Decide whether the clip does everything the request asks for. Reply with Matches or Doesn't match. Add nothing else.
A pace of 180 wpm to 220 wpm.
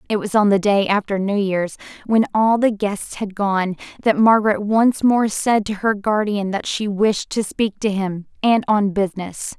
Matches